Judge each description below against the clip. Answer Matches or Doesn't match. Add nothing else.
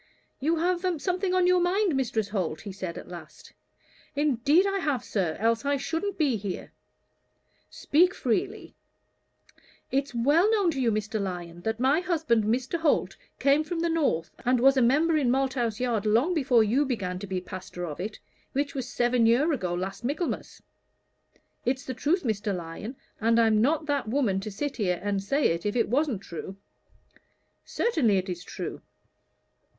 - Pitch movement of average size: Doesn't match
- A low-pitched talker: Doesn't match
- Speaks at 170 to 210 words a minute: Matches